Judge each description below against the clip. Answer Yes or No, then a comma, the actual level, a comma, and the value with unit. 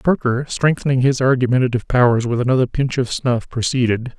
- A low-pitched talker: Yes, low, 125 Hz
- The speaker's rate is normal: Yes, average, 160 wpm